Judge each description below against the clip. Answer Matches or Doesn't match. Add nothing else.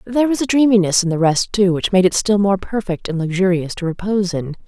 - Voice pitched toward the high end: Matches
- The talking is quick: Matches